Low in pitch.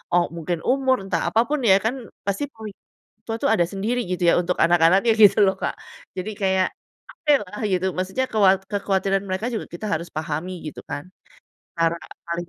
No: high, 195 Hz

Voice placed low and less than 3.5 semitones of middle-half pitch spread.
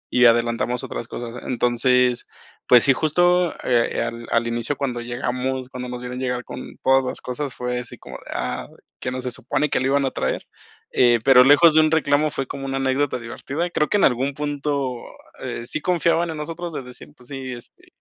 Yes: low, 130 Hz; average, 2.9 semitones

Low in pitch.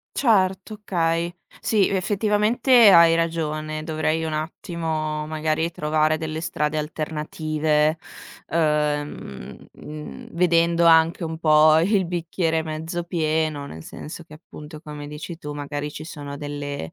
No: medium, 160 Hz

